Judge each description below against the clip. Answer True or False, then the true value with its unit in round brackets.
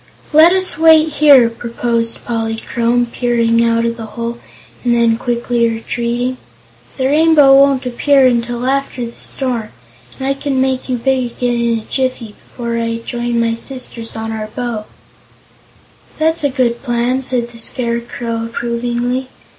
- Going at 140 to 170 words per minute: True (150 wpm)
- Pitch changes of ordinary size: False (2.1 semitones)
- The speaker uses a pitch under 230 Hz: False (240 Hz)